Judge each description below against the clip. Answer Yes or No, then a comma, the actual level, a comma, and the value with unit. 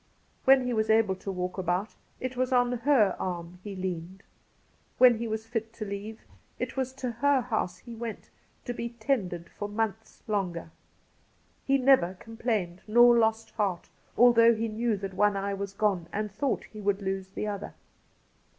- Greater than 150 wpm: Yes, average, 175 wpm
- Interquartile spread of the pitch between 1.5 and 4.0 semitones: Yes, average, 3.5 semitones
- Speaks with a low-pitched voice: No, high, 220 Hz